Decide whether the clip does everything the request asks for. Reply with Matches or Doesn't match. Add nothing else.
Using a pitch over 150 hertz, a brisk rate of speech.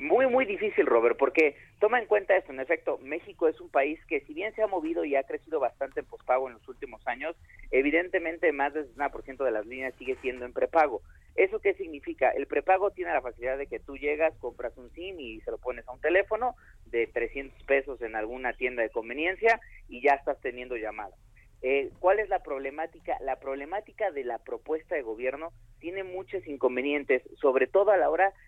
Matches